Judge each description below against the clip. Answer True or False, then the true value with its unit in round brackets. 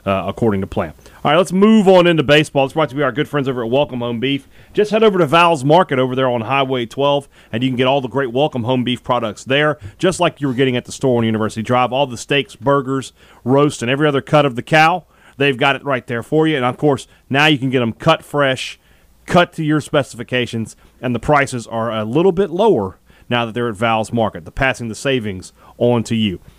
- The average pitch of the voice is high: False (130 Hz)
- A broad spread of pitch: False (4.1 semitones)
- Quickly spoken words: True (250 wpm)